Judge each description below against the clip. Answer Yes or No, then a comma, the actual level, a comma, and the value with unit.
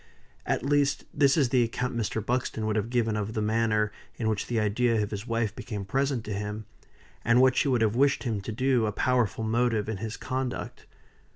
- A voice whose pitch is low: Yes, low, 115 Hz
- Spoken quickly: Yes, fast, 210 wpm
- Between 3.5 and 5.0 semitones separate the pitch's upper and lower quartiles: No, average, 2.8 semitones